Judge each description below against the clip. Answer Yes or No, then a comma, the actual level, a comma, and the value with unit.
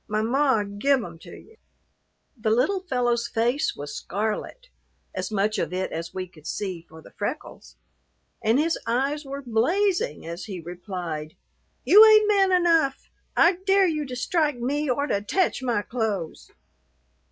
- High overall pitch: Yes, high, 245 Hz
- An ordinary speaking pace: Yes, average, 160 wpm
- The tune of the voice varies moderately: No, wide, 7.4 semitones